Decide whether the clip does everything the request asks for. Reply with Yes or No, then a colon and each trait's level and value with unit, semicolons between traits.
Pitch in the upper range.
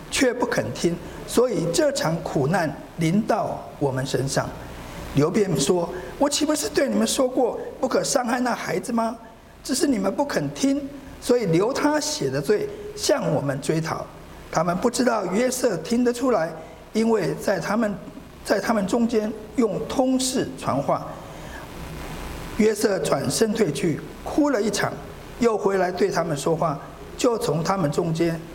Yes: high, 225 Hz